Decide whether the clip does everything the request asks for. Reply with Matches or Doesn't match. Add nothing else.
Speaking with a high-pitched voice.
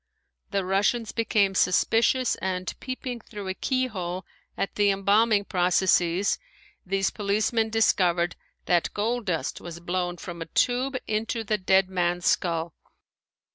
Matches